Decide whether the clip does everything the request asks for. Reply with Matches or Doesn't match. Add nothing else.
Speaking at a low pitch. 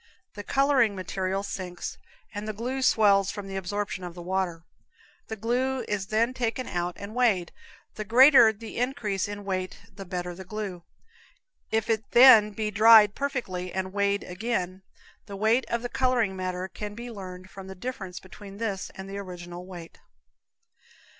Doesn't match